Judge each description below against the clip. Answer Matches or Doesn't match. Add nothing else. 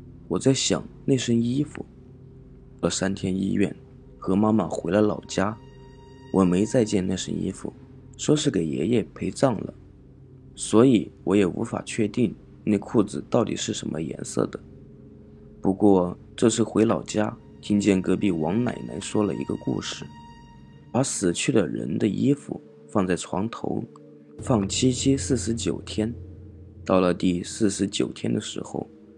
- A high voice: Doesn't match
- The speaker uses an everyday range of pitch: Matches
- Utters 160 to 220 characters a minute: Matches